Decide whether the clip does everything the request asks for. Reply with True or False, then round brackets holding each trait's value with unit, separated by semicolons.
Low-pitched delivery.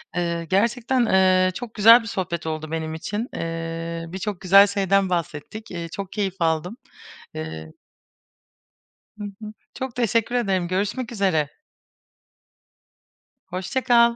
False (190 Hz)